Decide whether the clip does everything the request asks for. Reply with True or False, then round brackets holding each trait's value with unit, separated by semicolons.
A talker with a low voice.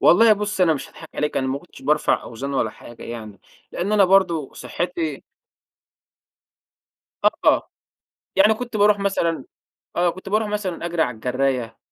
False (170 Hz)